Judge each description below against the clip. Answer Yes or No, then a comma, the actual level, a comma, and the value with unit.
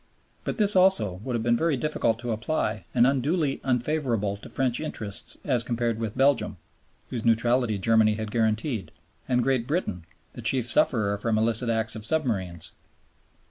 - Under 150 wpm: No, average, 160 wpm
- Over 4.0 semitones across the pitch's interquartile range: No, average, 3.5 semitones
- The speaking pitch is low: Yes, low, 115 Hz